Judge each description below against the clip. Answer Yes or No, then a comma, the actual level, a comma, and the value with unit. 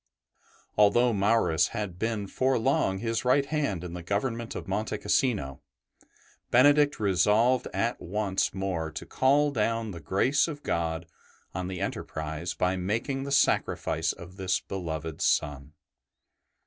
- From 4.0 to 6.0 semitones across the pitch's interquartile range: Yes, average, 5.3 semitones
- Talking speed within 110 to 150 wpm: Yes, average, 145 wpm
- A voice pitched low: Yes, low, 100 Hz